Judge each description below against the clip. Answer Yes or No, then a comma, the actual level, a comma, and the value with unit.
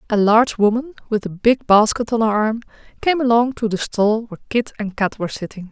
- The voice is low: No, high, 220 Hz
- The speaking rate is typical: No, fast, 220 wpm